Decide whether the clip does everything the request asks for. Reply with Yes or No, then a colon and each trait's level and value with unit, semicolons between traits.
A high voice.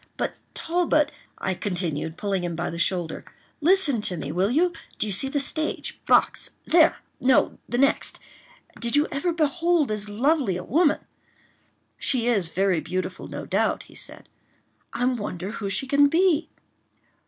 Yes: high, 240 Hz